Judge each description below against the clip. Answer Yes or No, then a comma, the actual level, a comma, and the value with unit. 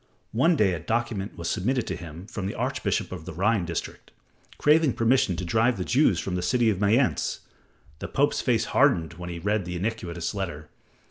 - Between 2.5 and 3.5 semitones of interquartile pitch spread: No, average, 5.2 semitones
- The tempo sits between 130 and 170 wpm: No, average, 195 wpm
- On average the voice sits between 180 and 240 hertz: No, low, 100 Hz